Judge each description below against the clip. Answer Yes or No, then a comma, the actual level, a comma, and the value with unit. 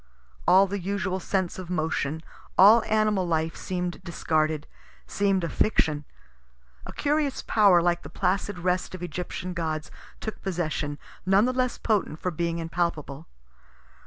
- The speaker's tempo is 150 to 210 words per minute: No, average, 140 wpm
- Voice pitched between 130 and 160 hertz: No, medium, 180 Hz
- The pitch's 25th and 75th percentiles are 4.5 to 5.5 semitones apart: No, average, 3.3 semitones